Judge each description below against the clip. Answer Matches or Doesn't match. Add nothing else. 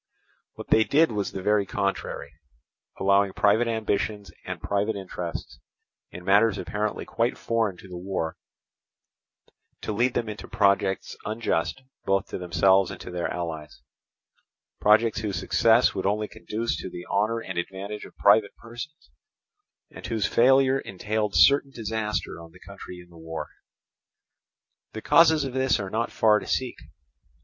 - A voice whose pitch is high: Doesn't match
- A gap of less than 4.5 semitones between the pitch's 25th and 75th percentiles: Matches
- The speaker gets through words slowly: Doesn't match